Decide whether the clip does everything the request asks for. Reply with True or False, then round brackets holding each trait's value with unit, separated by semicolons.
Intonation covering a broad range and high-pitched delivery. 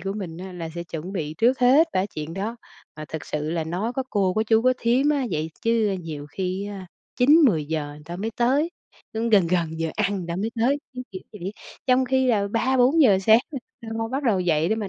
True (6.2 semitones; 200 Hz)